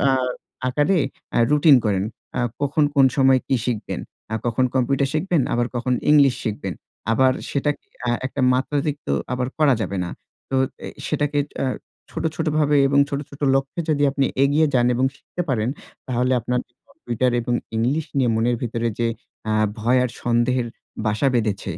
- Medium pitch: No, low, 130 Hz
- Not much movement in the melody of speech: No, average, 3.2 semitones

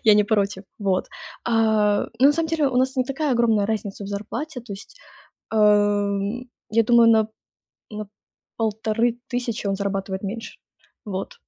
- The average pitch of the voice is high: Yes, high, 220 Hz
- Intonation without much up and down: No, average, 3.0 semitones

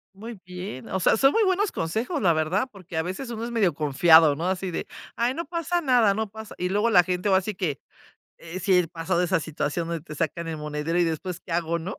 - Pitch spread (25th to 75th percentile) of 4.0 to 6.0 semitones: Yes, average, 5.0 semitones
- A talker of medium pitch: Yes, medium, 180 Hz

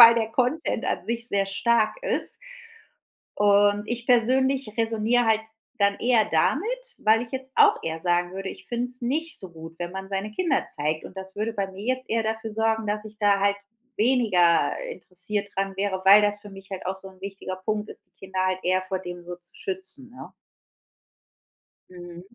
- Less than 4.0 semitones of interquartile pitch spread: Yes, average, 3.6 semitones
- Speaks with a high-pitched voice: Yes, high, 205 Hz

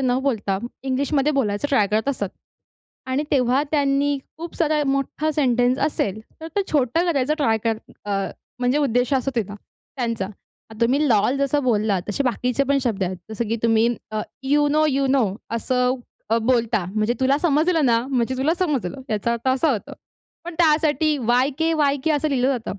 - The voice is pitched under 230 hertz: No, very high, 260 Hz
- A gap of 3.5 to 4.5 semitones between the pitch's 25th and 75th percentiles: Yes, average, 3.8 semitones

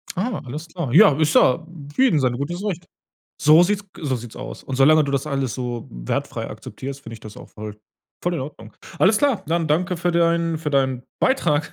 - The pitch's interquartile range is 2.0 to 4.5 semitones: No, average, 4.9 semitones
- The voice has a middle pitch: Yes, medium, 150 Hz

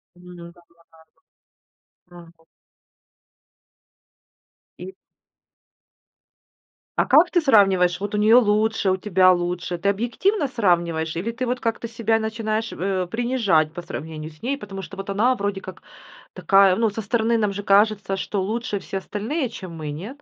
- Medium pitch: No, high, 200 Hz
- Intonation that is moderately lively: Yes, average, 4.1 semitones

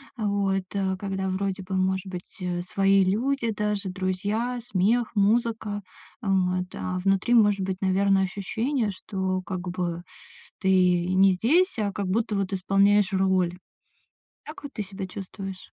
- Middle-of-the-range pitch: No, high, 195 Hz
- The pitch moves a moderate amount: No, narrow, 1.8 semitones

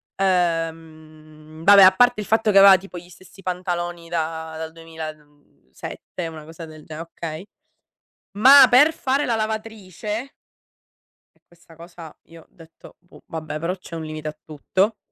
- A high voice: No, medium, 170 Hz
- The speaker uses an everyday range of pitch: Yes, average, 3.6 semitones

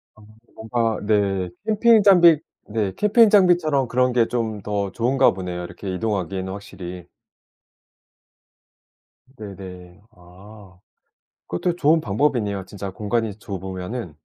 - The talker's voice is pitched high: No, low, 105 Hz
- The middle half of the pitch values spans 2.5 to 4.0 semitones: No, wide, 5.6 semitones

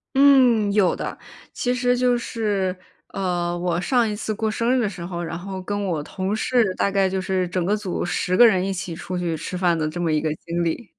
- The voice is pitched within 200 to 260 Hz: No, high, 190 Hz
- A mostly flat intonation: No, average, 3.8 semitones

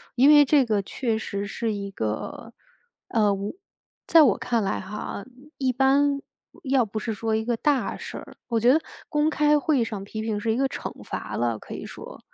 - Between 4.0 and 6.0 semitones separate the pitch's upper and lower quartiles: Yes, average, 4.7 semitones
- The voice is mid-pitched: No, high, 230 Hz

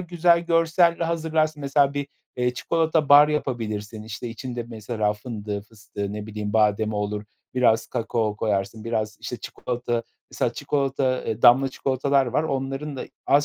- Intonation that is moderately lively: Yes, average, 4.9 semitones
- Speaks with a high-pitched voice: No, low, 125 Hz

